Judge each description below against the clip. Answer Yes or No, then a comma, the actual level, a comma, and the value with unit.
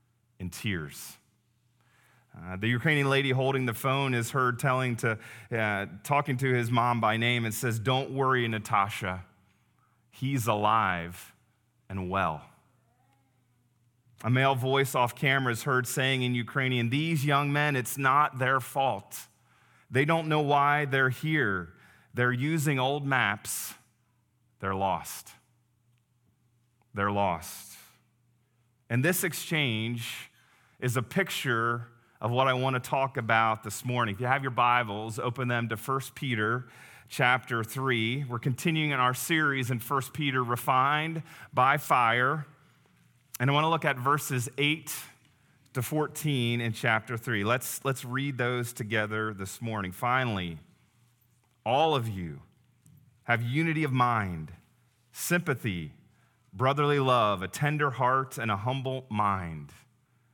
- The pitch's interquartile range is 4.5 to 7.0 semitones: No, average, 2.7 semitones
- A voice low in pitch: Yes, low, 125 Hz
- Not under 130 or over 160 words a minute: Yes, slow, 135 wpm